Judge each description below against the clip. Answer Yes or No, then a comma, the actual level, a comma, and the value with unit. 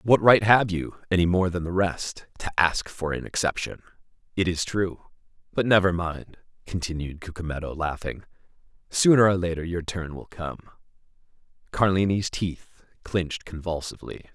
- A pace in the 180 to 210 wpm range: No, slow, 135 wpm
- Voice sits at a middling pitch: No, very low, 90 Hz